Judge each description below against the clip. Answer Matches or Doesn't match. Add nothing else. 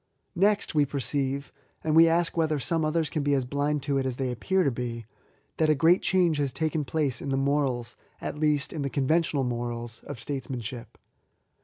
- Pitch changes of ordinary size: Matches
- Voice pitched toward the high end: Doesn't match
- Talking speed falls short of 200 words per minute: Doesn't match